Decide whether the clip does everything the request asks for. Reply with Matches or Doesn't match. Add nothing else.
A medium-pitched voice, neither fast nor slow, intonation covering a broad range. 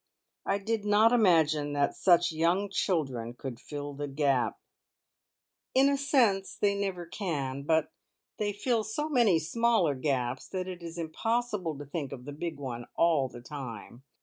Matches